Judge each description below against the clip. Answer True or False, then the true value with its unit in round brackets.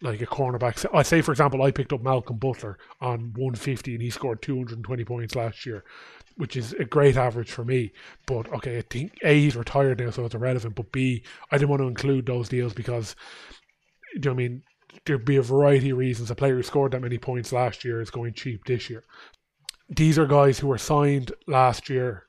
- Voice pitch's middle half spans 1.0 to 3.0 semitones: True (2.5 semitones)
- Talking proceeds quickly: True (225 wpm)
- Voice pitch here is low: True (130 Hz)